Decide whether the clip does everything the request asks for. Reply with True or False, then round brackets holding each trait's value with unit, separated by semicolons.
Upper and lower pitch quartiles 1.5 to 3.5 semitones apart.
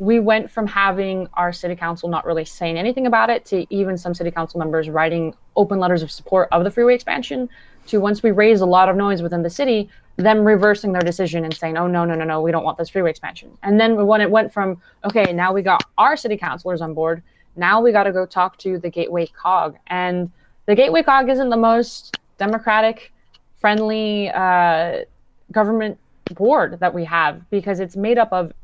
False (4.0 semitones)